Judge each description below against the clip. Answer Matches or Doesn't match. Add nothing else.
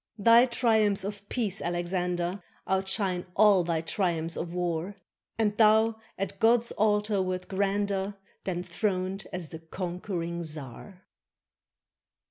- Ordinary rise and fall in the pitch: Matches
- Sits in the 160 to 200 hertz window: Matches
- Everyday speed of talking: Doesn't match